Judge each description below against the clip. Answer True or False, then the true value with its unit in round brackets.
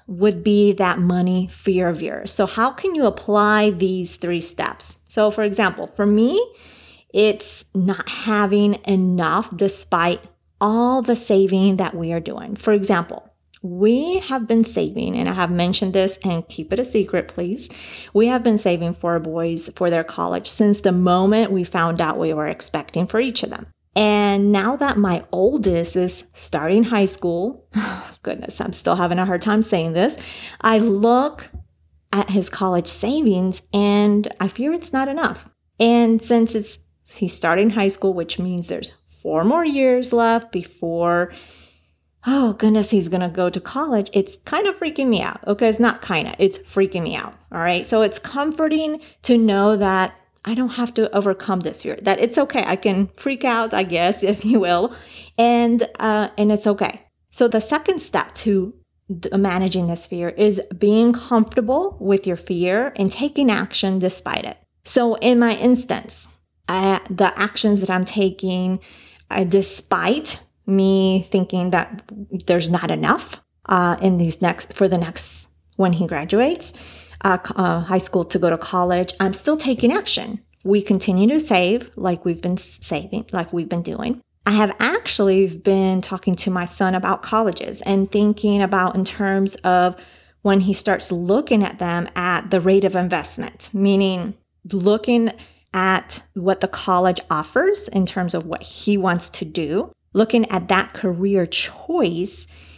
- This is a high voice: True (195 Hz)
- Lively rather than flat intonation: False (3.5 semitones)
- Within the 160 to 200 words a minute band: True (170 wpm)